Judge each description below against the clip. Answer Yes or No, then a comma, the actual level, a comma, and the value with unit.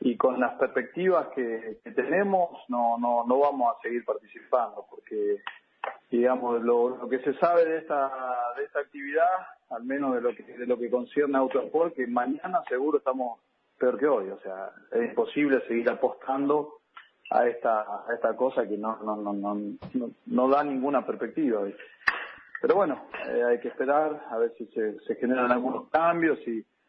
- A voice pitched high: No, low, 135 Hz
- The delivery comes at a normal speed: Yes, average, 180 wpm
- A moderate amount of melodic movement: No, wide, 5.8 semitones